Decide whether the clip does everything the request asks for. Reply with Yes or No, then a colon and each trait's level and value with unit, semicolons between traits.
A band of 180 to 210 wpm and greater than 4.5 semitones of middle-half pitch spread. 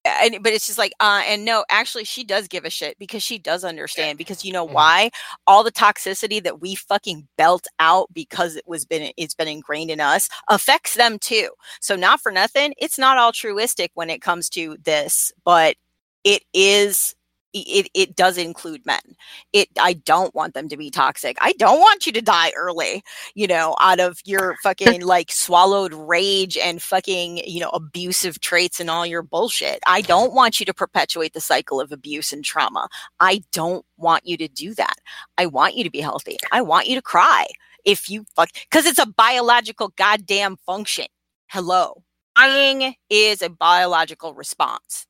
Yes: average, 190 wpm; average, 5.2 semitones